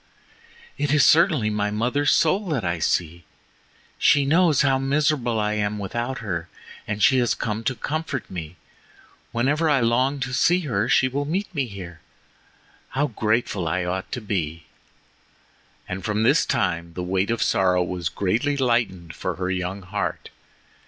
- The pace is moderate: Yes, average, 160 wpm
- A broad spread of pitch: Yes, wide, 7.0 semitones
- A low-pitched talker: Yes, low, 115 Hz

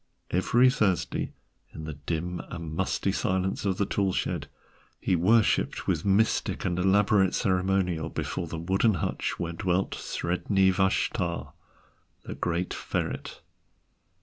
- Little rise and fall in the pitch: Yes, narrow, 2.1 semitones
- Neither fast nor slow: No, slow, 125 wpm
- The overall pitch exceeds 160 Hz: No, very low, 95 Hz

